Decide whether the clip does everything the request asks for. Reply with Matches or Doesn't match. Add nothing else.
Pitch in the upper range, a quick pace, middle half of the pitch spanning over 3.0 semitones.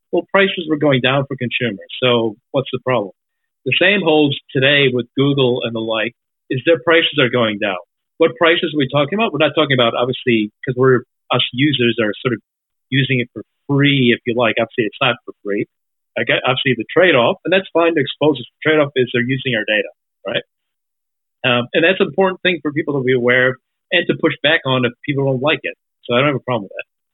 Doesn't match